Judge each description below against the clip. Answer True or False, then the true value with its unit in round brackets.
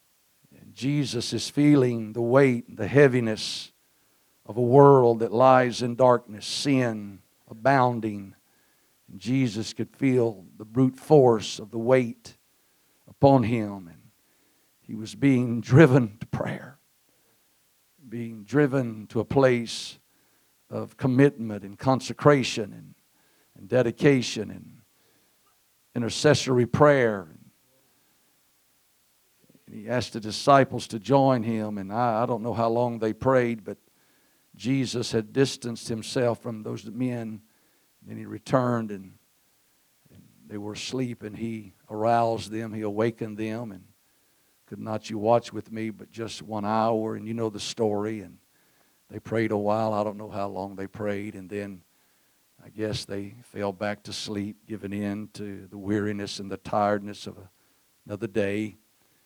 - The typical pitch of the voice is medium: False (115 Hz)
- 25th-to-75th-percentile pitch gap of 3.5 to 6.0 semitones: False (2.8 semitones)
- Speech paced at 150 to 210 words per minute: False (140 wpm)